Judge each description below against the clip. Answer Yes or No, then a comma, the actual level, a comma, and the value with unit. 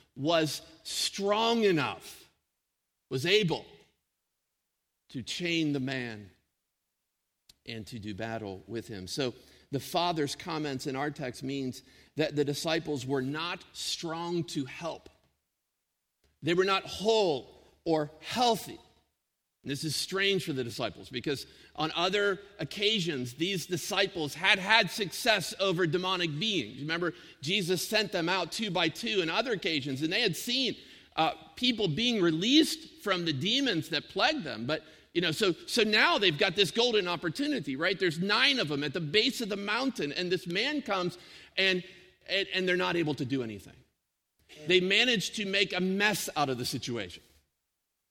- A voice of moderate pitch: Yes, medium, 175 Hz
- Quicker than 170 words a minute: No, average, 155 wpm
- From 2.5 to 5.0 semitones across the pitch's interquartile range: No, wide, 5.4 semitones